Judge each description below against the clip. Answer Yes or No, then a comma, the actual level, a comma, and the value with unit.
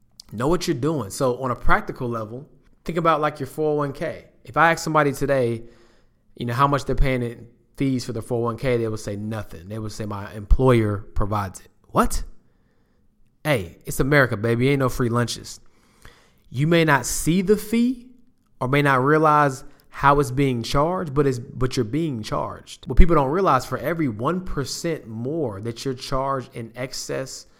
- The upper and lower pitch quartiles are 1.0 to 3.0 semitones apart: No, average, 4.4 semitones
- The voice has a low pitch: Yes, low, 130 Hz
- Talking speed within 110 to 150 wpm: No, average, 185 wpm